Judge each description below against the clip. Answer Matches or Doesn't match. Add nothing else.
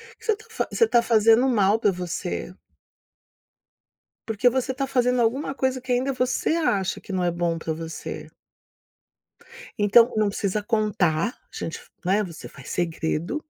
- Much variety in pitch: Matches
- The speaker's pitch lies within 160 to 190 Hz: Doesn't match